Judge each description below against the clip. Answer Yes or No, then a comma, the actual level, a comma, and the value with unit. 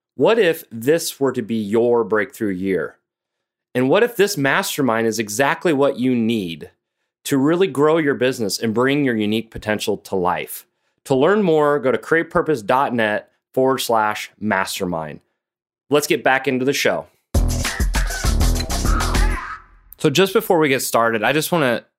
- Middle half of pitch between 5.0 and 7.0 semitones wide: Yes, average, 5.3 semitones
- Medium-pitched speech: No, low, 130 Hz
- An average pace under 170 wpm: Yes, average, 155 wpm